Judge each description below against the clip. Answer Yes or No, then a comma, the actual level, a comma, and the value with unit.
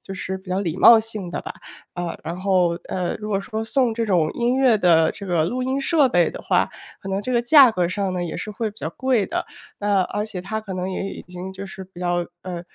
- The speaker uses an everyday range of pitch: Yes, average, 3.7 semitones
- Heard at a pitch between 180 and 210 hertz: Yes, high, 195 Hz